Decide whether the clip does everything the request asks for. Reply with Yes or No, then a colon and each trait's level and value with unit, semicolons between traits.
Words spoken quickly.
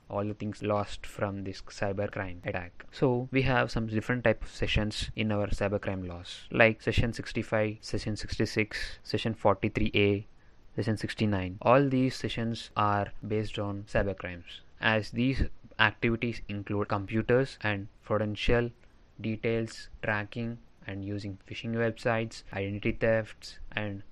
No: slow, 135 wpm